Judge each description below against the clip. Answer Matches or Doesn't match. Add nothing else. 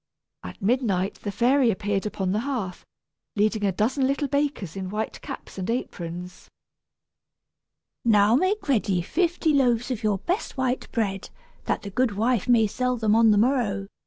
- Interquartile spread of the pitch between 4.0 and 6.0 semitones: Matches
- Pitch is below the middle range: Doesn't match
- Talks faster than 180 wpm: Doesn't match